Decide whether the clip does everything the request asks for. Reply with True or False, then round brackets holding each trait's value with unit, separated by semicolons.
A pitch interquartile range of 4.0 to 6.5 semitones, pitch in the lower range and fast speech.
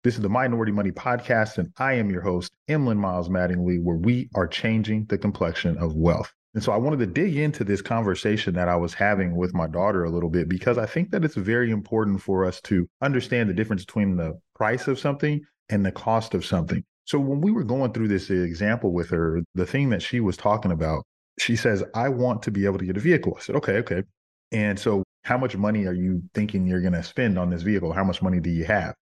True (4.8 semitones; 100 Hz; 240 wpm)